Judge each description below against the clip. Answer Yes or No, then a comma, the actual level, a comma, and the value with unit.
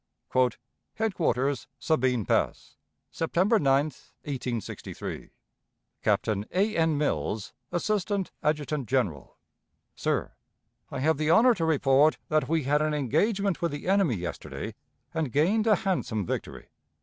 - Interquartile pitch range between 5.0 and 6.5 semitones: Yes, wide, 5.6 semitones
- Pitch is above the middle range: No, medium, 150 Hz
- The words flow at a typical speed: No, slow, 125 wpm